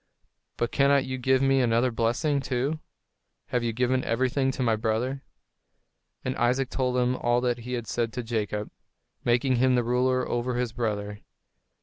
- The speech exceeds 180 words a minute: No, average, 170 wpm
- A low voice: Yes, low, 125 Hz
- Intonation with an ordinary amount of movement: No, narrow, 1.8 semitones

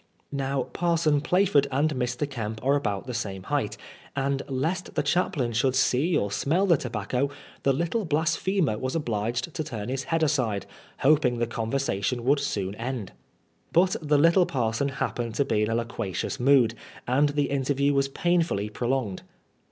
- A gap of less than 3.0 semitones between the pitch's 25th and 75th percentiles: No, average, 4.2 semitones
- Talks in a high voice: No, low, 135 Hz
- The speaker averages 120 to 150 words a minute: No, average, 165 wpm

